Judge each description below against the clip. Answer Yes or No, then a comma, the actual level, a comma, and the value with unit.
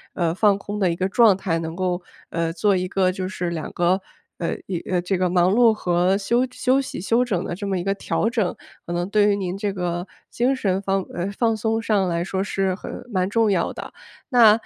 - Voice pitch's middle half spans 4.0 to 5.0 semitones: No, average, 2.9 semitones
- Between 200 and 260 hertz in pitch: No, high, 190 Hz